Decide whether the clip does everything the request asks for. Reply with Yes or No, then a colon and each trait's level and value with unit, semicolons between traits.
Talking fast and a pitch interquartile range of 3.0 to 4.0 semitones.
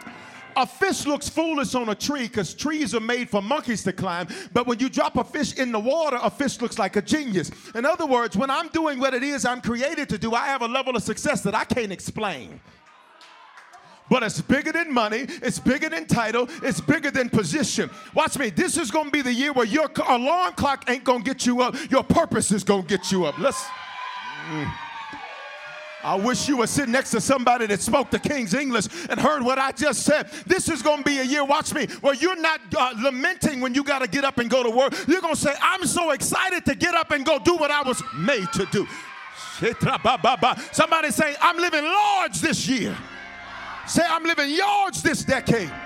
No: fast, 215 wpm; average, 4.6 semitones